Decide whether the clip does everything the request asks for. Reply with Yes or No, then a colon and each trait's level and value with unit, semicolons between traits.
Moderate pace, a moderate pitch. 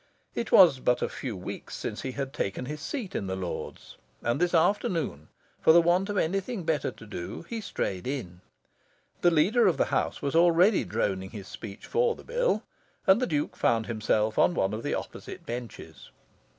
Yes: average, 190 wpm; medium, 150 Hz